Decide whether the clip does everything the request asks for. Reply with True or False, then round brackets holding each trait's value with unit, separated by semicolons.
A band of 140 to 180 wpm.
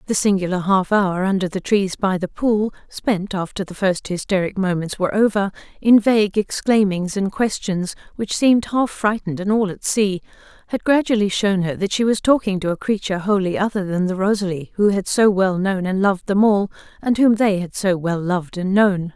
False (205 wpm)